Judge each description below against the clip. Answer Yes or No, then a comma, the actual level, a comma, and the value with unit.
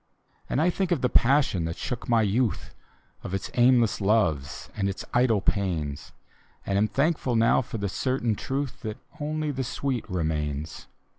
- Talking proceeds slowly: No, average, 165 wpm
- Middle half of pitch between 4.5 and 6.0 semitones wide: Yes, average, 5.3 semitones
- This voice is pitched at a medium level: No, low, 115 Hz